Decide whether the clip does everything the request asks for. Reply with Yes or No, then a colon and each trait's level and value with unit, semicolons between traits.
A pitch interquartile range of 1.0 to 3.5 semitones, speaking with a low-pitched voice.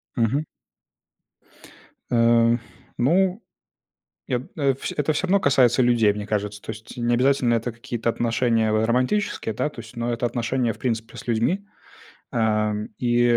Yes: narrow, 2.4 semitones; low, 120 Hz